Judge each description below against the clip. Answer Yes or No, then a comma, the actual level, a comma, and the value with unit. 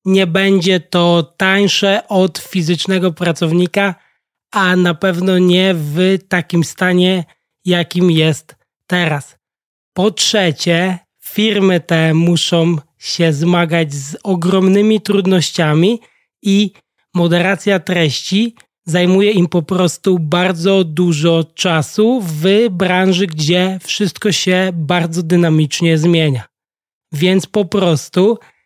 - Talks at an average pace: No, slow, 100 wpm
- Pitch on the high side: No, medium, 180 Hz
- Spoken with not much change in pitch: Yes, narrow, 2.2 semitones